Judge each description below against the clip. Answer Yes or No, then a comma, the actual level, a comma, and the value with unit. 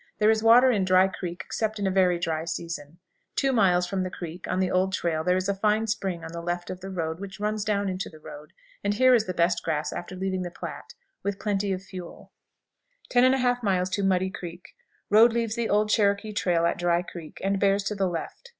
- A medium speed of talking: No, fast, 225 wpm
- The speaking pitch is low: No, high, 190 Hz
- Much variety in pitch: No, average, 3.0 semitones